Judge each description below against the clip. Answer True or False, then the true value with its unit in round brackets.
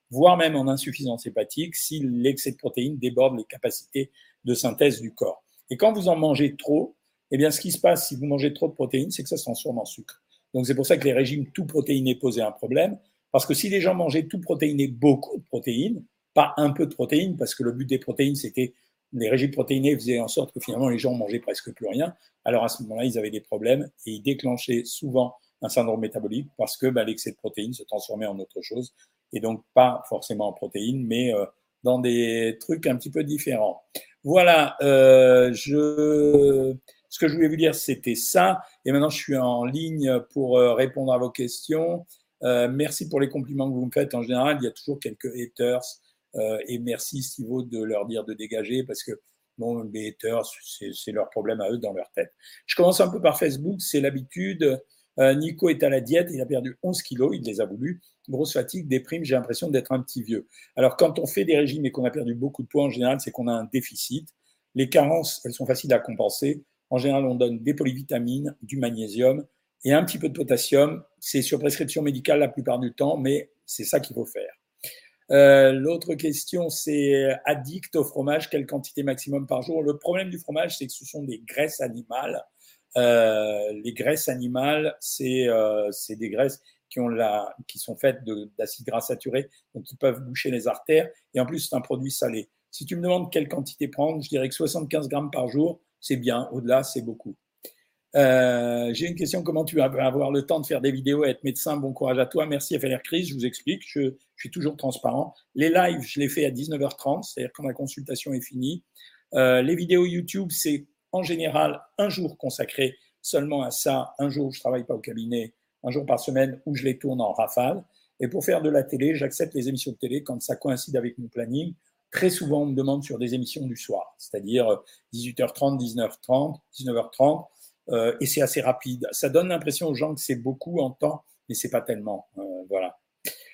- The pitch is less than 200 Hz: True (135 Hz)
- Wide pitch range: False (3.2 semitones)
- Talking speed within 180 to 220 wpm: True (215 wpm)